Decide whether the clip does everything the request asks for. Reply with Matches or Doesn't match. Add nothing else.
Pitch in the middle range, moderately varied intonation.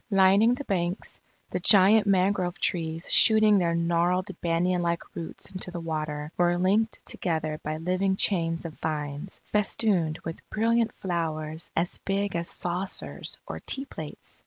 Matches